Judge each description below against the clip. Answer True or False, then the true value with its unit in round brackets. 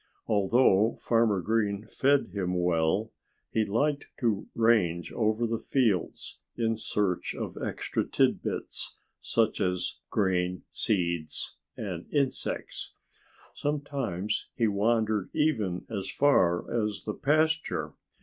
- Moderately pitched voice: False (105 Hz)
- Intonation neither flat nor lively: True (4.3 semitones)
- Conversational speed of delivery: False (110 wpm)